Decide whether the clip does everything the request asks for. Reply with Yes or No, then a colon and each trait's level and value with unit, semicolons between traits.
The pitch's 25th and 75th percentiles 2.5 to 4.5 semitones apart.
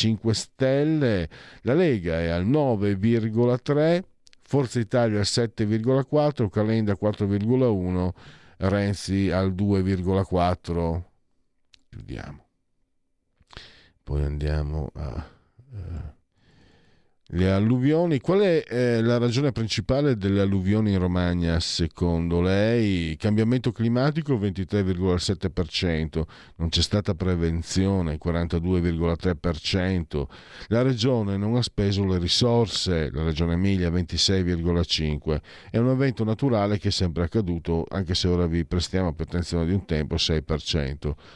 No: average, 5.1 semitones